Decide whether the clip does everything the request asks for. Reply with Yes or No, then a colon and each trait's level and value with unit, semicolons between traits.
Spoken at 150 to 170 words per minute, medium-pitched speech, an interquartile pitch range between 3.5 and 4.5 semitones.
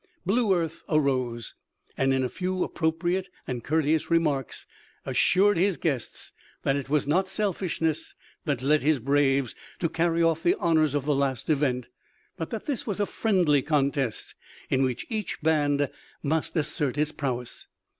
Yes: average, 155 wpm; medium, 155 Hz; average, 3.9 semitones